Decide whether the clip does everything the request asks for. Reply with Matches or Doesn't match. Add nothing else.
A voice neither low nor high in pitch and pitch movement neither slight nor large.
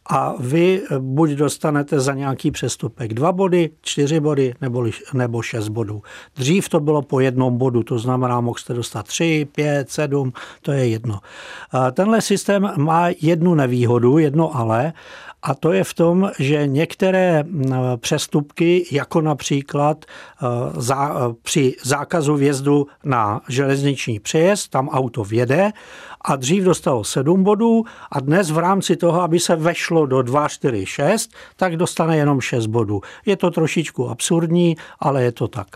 Matches